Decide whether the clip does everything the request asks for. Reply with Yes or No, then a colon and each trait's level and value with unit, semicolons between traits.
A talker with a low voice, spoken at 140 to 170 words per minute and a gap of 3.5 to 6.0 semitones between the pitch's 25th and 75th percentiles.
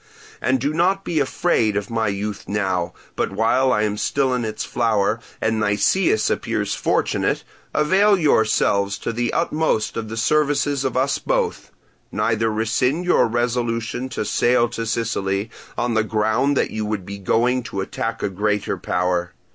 Yes: low, 115 Hz; average, 165 wpm; average, 3.9 semitones